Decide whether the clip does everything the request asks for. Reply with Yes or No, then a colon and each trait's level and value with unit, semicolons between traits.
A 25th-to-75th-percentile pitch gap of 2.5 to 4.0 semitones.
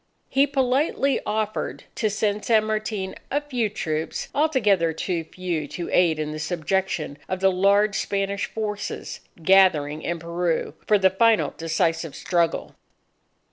No: average, 4.4 semitones